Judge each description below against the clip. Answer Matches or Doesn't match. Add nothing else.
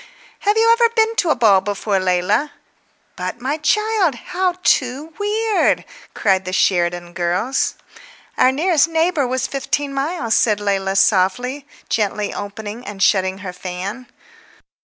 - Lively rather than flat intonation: Matches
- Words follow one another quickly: Doesn't match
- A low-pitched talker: Doesn't match